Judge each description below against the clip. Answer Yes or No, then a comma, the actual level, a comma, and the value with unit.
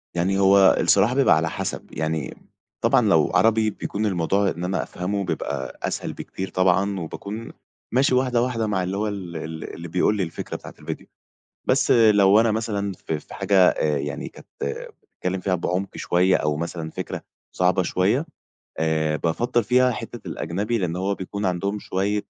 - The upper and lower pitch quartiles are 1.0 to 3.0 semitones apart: No, average, 3.6 semitones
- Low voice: Yes, very low, 95 Hz